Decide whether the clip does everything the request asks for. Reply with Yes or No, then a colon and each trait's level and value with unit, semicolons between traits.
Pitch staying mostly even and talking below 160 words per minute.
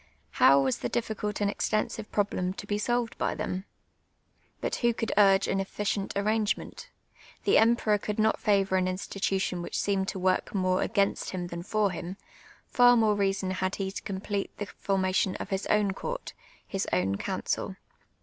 No: narrow, 2.0 semitones; average, 175 wpm